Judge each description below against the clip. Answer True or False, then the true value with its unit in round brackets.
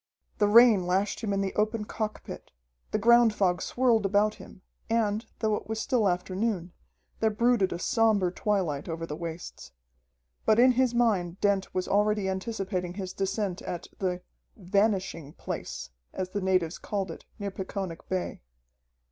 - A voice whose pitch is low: False (200 Hz)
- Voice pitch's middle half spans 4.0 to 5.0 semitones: False (3.0 semitones)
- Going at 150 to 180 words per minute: True (155 wpm)